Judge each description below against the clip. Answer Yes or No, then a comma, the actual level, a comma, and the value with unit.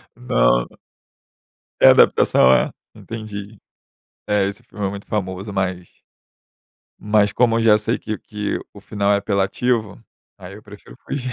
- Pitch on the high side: No, low, 100 Hz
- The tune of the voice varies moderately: No, narrow, 1.9 semitones